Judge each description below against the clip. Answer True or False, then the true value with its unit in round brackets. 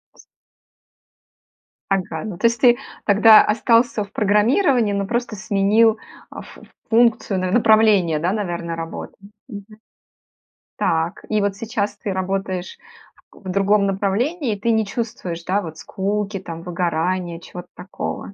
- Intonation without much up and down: False (3.4 semitones)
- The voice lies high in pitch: True (200 Hz)